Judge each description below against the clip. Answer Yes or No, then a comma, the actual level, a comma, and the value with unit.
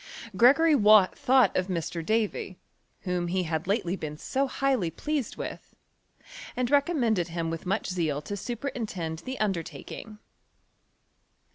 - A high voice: Yes, high, 200 Hz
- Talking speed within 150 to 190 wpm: No, slow, 135 wpm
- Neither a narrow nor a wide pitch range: No, wide, 6.7 semitones